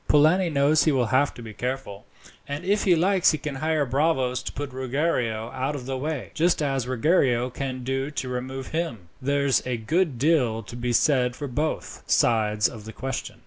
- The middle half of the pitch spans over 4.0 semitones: No, average, 3.6 semitones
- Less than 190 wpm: No, average, 195 wpm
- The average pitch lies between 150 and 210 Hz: No, low, 135 Hz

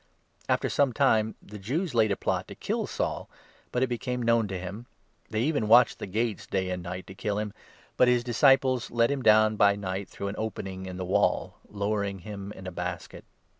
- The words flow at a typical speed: No, fast, 220 wpm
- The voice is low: Yes, low, 105 Hz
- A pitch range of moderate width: Yes, average, 3.7 semitones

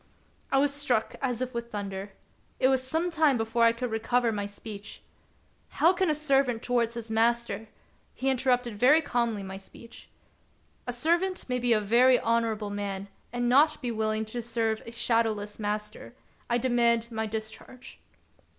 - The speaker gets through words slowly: No, average, 180 wpm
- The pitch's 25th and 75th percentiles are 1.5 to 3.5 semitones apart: Yes, average, 2.7 semitones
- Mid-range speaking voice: No, high, 235 Hz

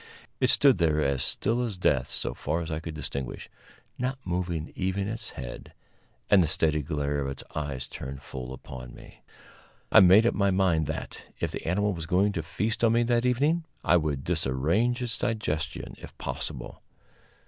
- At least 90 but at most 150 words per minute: No, average, 180 wpm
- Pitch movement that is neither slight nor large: No, wide, 6.5 semitones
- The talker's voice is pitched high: No, very low, 85 Hz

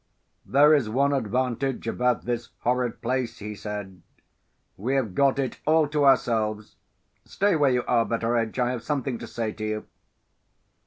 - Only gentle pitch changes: No, average, 3.3 semitones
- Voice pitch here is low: Yes, low, 125 Hz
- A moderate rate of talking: Yes, average, 160 wpm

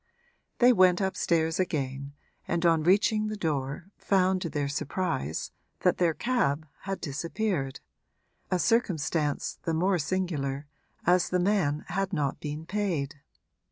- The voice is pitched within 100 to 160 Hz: No, medium, 170 Hz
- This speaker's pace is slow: Yes, slow, 130 wpm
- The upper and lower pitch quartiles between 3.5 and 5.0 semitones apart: Yes, average, 4.5 semitones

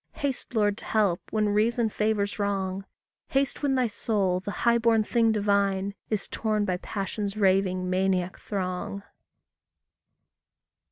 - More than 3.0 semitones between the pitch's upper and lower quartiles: No, narrow, 2.4 semitones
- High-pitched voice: Yes, high, 205 Hz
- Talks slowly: Yes, slow, 130 wpm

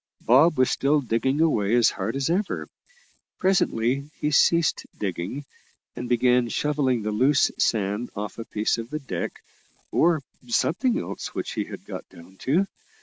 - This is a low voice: Yes, low, 130 Hz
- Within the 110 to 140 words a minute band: No, average, 155 wpm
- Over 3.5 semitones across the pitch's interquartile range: Yes, average, 5.0 semitones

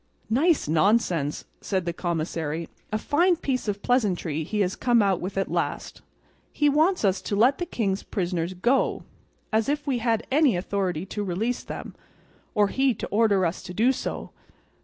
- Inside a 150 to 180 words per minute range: Yes, average, 175 wpm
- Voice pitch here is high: Yes, high, 205 Hz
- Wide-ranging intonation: Yes, wide, 5.8 semitones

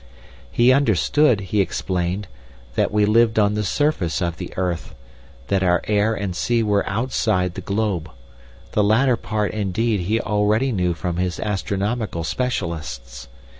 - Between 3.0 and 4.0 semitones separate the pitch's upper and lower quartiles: Yes, average, 3.6 semitones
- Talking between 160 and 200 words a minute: No, average, 145 wpm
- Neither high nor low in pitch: No, low, 100 Hz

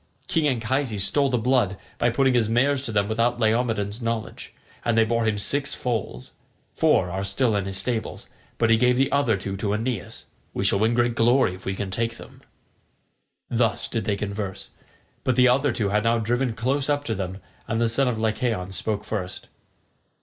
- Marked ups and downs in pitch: No, average, 3.3 semitones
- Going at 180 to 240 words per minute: Yes, average, 195 wpm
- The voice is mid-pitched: No, low, 115 Hz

